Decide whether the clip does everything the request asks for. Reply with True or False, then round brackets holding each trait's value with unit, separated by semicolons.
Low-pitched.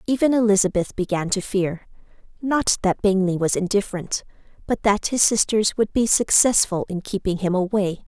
False (200 Hz)